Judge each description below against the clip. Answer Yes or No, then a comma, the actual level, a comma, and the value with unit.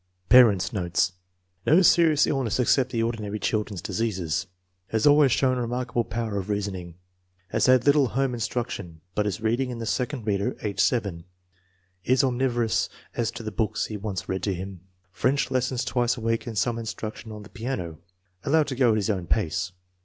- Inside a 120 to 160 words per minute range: No, average, 190 wpm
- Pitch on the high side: No, low, 115 Hz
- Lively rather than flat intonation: No, average, 4.1 semitones